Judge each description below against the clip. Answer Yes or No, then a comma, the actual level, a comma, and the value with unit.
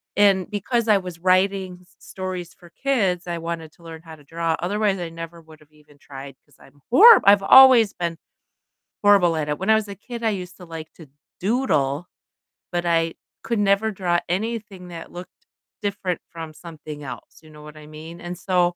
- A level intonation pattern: No, average, 3.5 semitones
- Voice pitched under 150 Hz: No, medium, 175 Hz